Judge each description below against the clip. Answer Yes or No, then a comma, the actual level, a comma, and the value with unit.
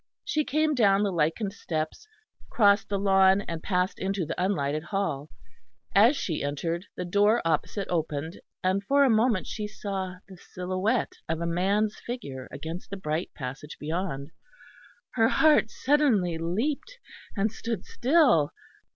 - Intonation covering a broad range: No, average, 4.8 semitones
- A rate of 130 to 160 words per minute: Yes, average, 145 wpm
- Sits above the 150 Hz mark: Yes, high, 190 Hz